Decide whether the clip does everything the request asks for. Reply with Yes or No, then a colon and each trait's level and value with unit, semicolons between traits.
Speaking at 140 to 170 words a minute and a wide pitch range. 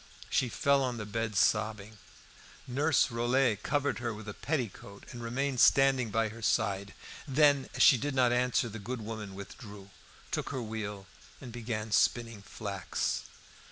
No: average, 155 wpm; average, 3.4 semitones